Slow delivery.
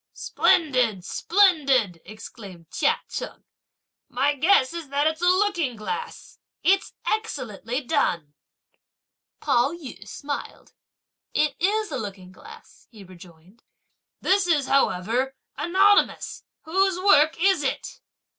Yes: slow, 110 wpm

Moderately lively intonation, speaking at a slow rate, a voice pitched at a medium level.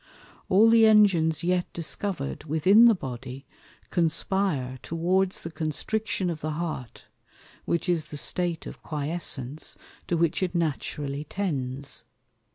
Yes: average, 4.2 semitones; slow, 125 wpm; medium, 165 Hz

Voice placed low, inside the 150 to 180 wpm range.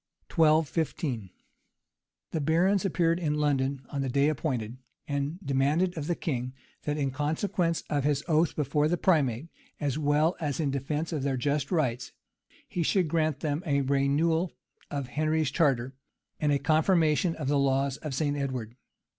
No: medium, 150 Hz; average, 165 wpm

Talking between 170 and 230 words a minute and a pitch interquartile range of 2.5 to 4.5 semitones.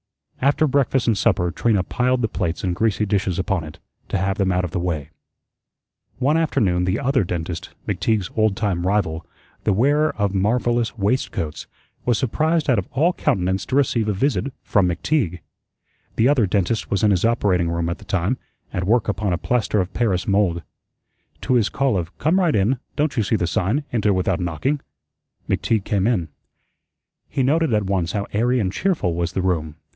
No: average, 190 wpm; wide, 5.4 semitones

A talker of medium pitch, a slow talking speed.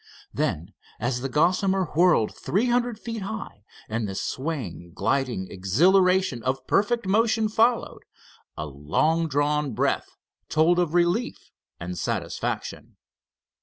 Yes: medium, 160 Hz; slow, 120 wpm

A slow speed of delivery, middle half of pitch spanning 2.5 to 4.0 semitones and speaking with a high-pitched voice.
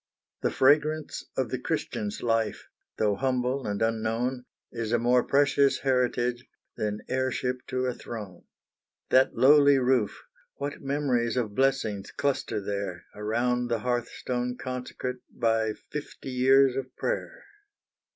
No: slow, 125 wpm; average, 2.9 semitones; low, 125 Hz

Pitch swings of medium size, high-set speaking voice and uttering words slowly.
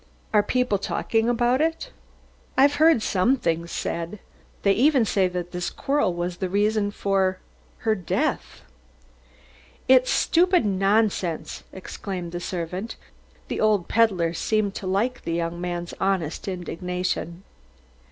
Yes: average, 4.4 semitones; high, 195 Hz; slow, 130 wpm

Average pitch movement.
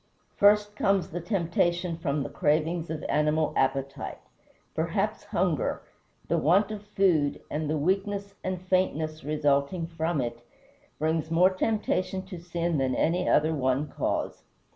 Yes: average, 3.7 semitones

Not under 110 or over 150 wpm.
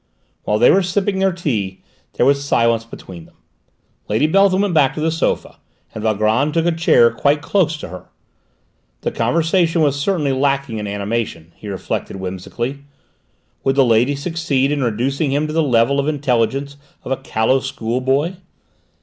No: average, 165 wpm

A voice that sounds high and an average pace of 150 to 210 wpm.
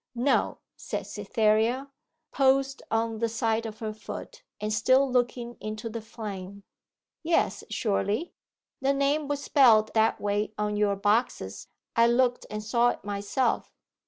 No: high, 225 Hz; average, 140 wpm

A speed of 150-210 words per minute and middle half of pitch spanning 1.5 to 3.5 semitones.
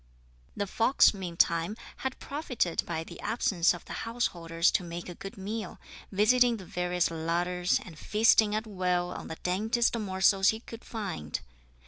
No: average, 155 wpm; average, 4.1 semitones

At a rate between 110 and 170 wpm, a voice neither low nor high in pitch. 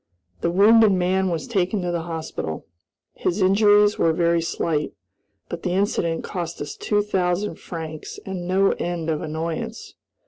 Yes: average, 150 wpm; medium, 175 Hz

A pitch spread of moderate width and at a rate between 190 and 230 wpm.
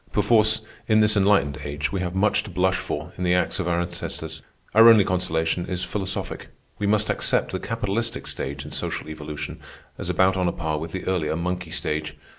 Yes: average, 4.2 semitones; average, 200 wpm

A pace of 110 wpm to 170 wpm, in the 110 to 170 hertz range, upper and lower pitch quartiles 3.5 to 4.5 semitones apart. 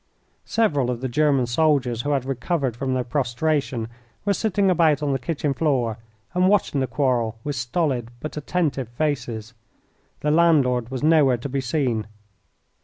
Yes: average, 160 wpm; low, 135 Hz; average, 3.9 semitones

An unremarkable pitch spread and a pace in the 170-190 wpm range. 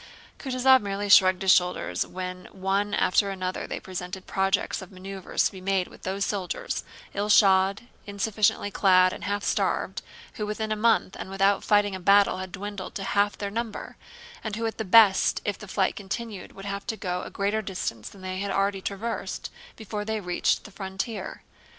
No: narrow, 1.8 semitones; average, 180 wpm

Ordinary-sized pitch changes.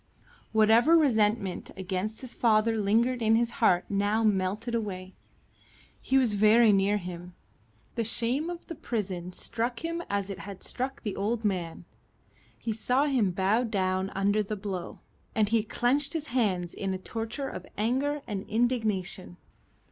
Yes: average, 3.6 semitones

